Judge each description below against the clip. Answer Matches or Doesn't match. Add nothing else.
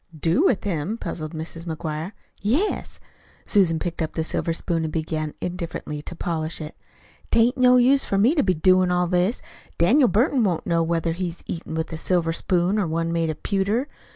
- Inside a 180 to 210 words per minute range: Matches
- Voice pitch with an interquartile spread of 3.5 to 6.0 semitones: Matches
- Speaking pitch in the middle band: Matches